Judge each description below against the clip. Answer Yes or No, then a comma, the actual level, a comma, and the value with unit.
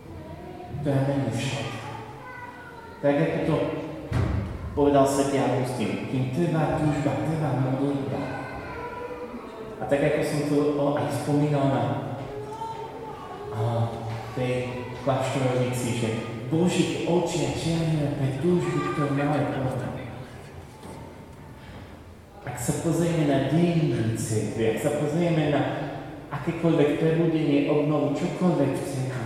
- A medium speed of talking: No, slow, 105 wpm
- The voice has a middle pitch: Yes, medium, 145 Hz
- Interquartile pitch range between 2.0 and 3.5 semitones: Yes, average, 3.1 semitones